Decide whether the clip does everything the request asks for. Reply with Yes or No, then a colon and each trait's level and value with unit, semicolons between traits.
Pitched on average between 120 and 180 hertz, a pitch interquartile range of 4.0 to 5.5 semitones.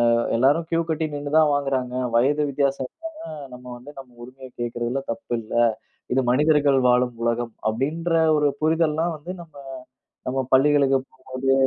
No: low, 135 Hz; average, 3.1 semitones